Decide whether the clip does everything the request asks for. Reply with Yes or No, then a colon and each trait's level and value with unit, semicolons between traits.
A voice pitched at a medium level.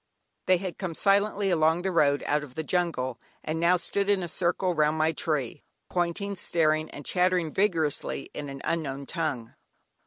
Yes: medium, 165 Hz